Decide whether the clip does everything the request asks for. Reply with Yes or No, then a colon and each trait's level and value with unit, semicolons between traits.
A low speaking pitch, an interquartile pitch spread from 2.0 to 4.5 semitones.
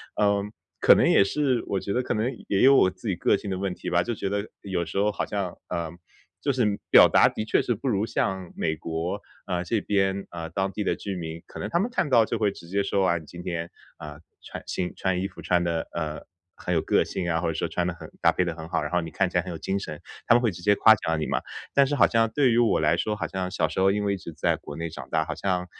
Yes: very low, 95 Hz; average, 3.5 semitones